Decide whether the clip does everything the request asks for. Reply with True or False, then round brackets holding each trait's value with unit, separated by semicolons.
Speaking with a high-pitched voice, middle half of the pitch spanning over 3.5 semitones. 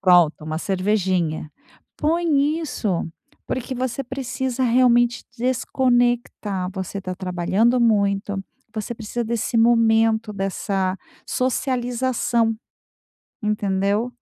True (225 Hz; 4.2 semitones)